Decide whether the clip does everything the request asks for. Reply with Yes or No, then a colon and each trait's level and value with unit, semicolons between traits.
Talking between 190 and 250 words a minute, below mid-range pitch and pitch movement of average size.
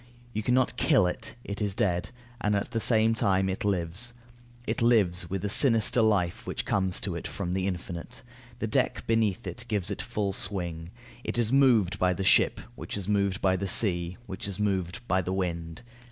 Yes: average, 200 wpm; low, 100 Hz; average, 3.2 semitones